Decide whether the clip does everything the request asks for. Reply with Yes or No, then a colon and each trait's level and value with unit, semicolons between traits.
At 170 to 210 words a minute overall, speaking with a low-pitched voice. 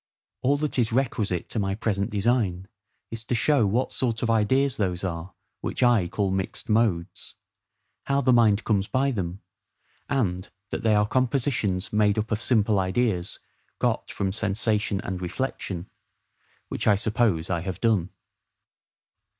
No: average, 150 wpm; low, 105 Hz